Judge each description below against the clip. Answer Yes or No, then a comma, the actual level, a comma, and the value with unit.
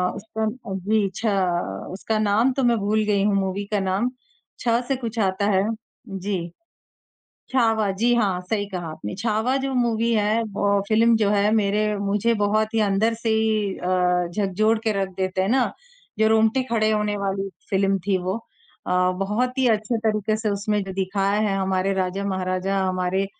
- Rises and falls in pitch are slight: Yes, narrow, 2.2 semitones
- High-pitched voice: Yes, high, 210 Hz